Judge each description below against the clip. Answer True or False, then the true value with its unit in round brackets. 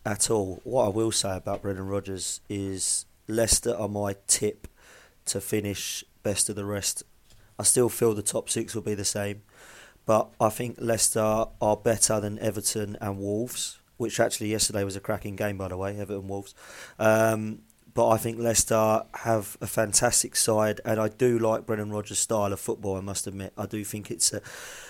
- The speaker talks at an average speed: True (190 wpm)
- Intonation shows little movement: True (2.0 semitones)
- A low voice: True (105 Hz)